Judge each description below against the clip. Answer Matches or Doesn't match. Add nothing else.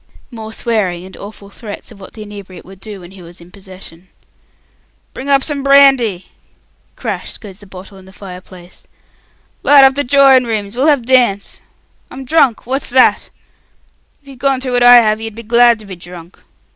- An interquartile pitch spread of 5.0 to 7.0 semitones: Matches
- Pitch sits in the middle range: Doesn't match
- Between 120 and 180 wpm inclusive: Doesn't match